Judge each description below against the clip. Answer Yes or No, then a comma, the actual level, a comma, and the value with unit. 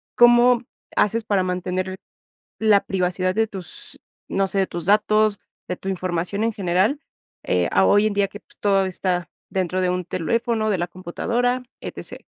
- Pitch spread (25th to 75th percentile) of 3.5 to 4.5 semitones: No, average, 3.0 semitones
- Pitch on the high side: Yes, high, 195 Hz